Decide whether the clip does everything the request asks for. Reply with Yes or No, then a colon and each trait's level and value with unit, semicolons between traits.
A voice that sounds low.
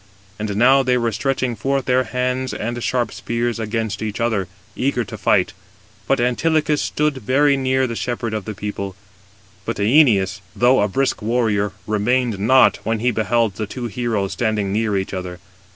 Yes: low, 115 Hz